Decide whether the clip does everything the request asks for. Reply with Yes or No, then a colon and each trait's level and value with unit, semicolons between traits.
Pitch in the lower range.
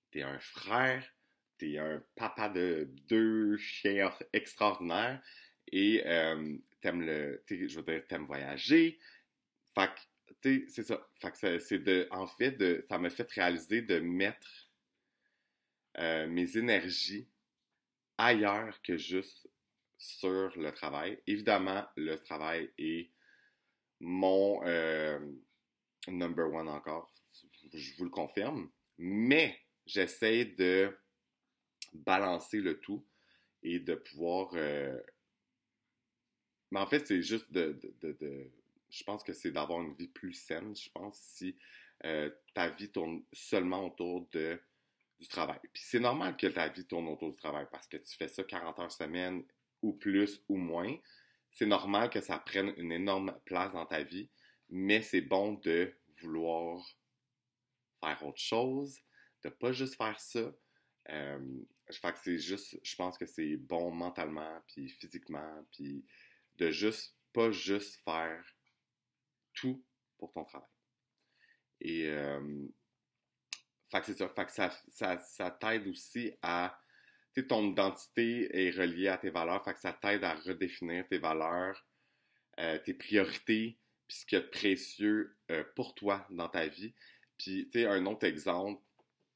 Yes: very low, 95 Hz